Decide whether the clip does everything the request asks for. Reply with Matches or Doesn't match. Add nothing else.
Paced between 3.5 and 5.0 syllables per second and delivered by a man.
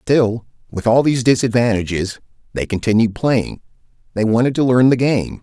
Doesn't match